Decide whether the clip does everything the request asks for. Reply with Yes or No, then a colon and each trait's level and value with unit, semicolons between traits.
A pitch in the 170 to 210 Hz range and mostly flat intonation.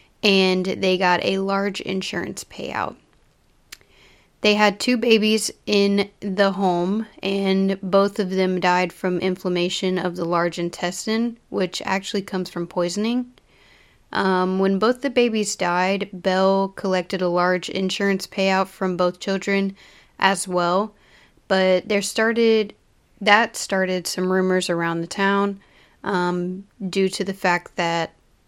Yes: high, 190 Hz; narrow, 1.6 semitones